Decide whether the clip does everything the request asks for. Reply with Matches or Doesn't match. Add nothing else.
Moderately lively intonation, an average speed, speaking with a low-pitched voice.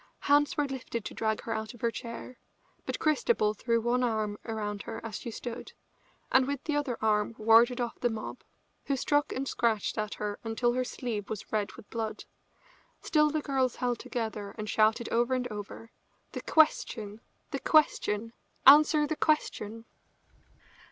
Doesn't match